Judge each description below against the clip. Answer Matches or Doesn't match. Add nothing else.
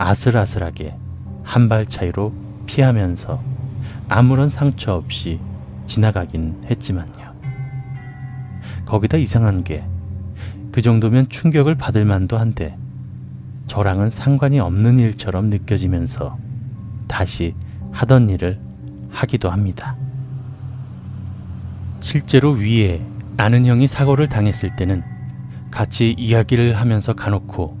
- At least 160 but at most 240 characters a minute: Matches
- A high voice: Doesn't match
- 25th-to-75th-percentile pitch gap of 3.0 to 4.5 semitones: Matches